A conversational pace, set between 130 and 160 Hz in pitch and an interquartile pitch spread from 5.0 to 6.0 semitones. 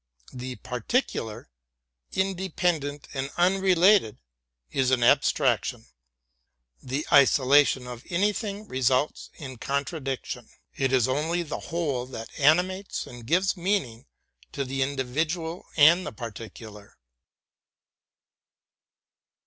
No: slow, 110 wpm; medium, 140 Hz; wide, 5.6 semitones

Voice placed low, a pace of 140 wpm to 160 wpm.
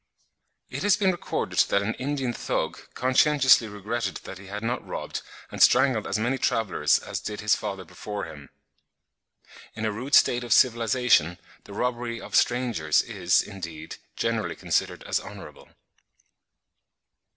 Yes: low, 110 Hz; average, 145 wpm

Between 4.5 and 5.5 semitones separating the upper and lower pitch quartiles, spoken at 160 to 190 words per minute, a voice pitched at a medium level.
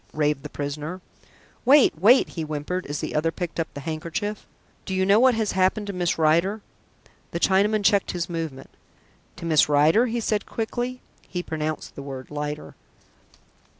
Yes: average, 5.2 semitones; average, 170 wpm; medium, 170 Hz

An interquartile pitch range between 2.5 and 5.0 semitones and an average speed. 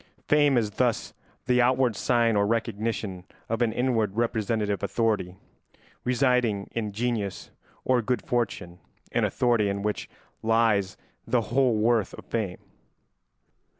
No: average, 2.9 semitones; slow, 125 wpm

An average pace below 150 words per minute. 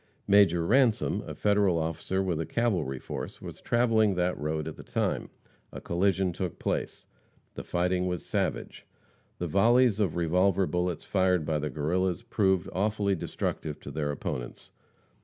No: average, 155 wpm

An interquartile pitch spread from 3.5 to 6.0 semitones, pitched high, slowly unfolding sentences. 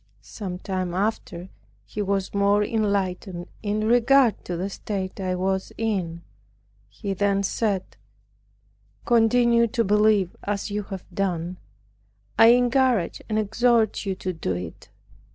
No: average, 3.1 semitones; high, 200 Hz; slow, 130 wpm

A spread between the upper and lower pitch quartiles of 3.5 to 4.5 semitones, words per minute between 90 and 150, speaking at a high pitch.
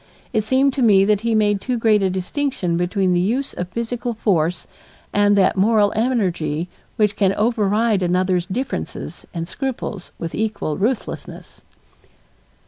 Yes: average, 3.9 semitones; average, 145 wpm; high, 205 Hz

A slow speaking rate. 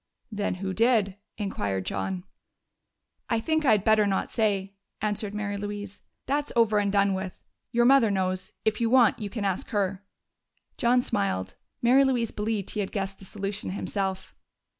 No: average, 165 wpm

